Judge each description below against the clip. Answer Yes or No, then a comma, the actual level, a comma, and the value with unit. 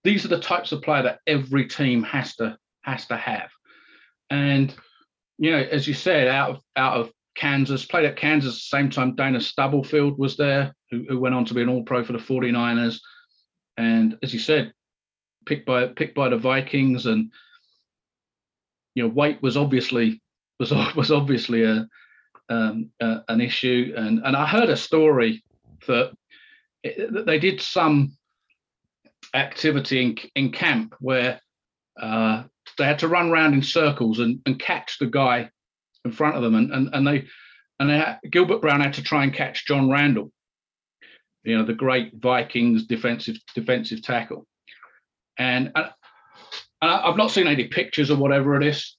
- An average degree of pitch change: Yes, average, 3.7 semitones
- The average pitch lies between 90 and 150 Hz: Yes, low, 135 Hz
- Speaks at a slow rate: No, average, 170 wpm